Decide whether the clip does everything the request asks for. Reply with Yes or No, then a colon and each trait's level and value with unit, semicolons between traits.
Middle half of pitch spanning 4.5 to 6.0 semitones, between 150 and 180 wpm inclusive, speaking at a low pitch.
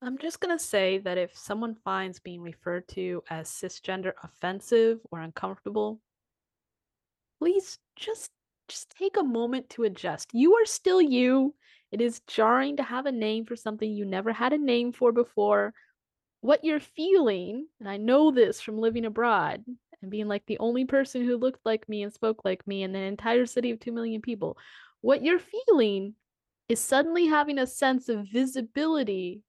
No: average, 5.0 semitones; average, 175 wpm; high, 235 Hz